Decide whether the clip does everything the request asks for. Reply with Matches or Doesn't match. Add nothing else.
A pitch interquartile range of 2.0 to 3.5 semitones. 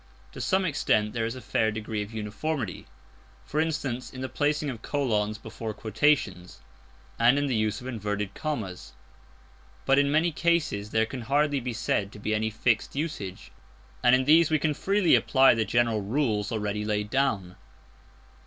Doesn't match